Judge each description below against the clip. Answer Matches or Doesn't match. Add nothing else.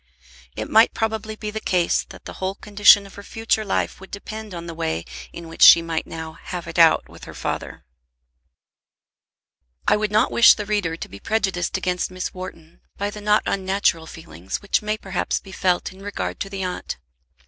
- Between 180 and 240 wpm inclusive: Matches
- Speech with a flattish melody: Doesn't match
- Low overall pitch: Doesn't match